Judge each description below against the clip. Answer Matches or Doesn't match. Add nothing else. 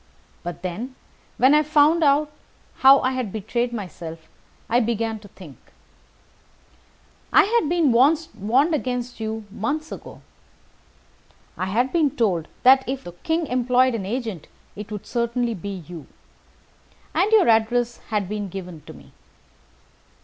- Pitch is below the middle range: Doesn't match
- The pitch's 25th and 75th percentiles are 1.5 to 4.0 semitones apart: Doesn't match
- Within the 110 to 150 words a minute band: Matches